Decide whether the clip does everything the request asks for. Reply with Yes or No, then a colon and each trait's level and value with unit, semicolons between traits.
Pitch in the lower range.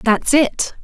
No: very high, 260 Hz